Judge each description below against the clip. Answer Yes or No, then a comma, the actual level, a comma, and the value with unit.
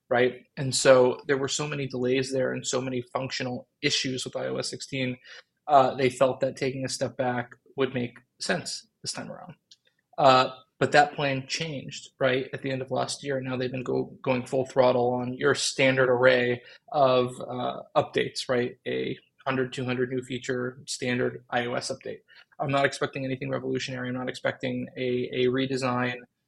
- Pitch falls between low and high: No, low, 130 Hz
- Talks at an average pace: Yes, average, 175 wpm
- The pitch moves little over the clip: Yes, narrow, 1.2 semitones